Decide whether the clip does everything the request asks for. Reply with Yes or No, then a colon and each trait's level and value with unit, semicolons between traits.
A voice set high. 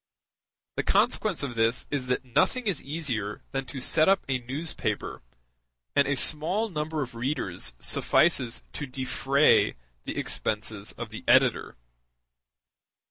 No: low, 135 Hz